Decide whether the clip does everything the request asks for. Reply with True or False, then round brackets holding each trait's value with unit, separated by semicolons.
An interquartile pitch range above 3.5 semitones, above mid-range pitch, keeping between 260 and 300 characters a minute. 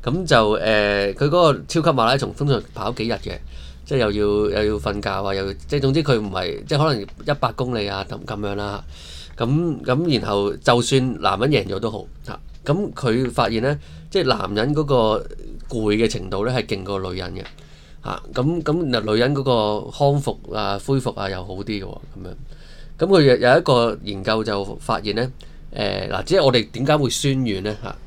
False (5.1 semitones; 110 Hz; 285 characters per minute)